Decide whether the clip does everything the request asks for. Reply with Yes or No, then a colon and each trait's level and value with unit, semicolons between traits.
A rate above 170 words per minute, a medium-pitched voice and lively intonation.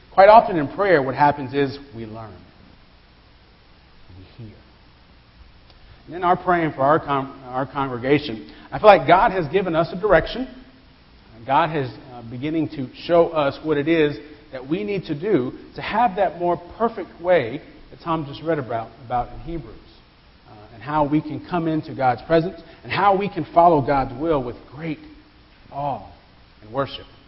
Yes: average, 180 wpm; medium, 145 Hz; wide, 6.2 semitones